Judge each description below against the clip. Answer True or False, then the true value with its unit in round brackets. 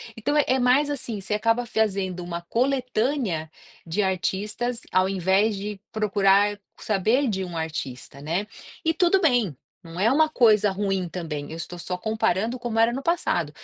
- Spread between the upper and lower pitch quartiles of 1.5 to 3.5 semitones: False (5.0 semitones)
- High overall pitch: True (210 Hz)